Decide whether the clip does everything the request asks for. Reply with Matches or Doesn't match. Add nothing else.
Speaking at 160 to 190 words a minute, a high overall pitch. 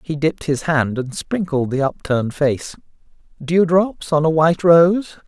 Doesn't match